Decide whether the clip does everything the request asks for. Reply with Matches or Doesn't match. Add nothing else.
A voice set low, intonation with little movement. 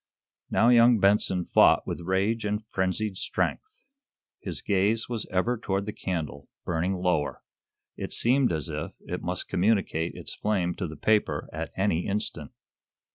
Doesn't match